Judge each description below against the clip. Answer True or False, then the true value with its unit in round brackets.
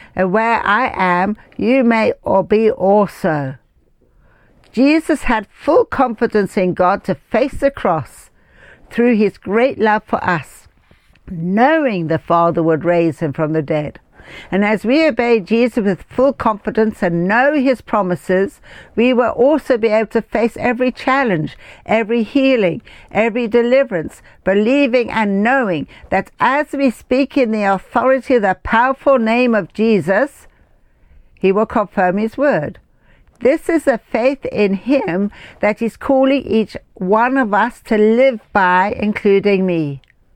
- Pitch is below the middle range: False (220 Hz)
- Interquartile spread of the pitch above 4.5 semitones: True (5.1 semitones)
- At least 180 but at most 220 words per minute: False (145 wpm)